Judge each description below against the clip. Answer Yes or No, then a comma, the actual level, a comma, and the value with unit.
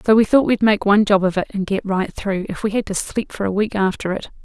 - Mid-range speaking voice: No, high, 200 Hz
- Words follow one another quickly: Yes, fast, 310 wpm